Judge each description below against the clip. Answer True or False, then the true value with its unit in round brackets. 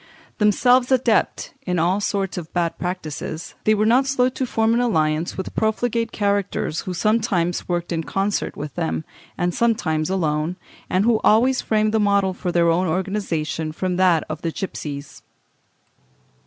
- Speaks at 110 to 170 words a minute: True (160 wpm)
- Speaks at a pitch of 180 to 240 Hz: True (190 Hz)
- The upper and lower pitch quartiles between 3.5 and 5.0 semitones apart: True (4.6 semitones)